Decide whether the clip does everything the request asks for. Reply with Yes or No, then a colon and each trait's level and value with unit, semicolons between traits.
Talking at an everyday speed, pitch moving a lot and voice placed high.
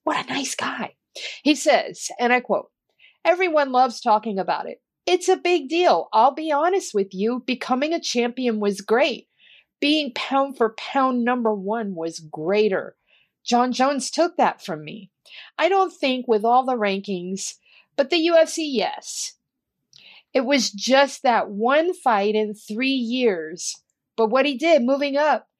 Yes: average, 160 wpm; wide, 5.7 semitones; very high, 255 Hz